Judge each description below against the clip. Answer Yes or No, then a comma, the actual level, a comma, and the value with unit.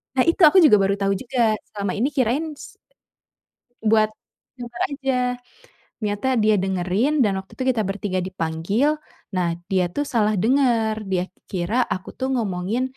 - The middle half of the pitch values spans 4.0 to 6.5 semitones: Yes, average, 5.0 semitones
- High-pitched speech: Yes, high, 215 Hz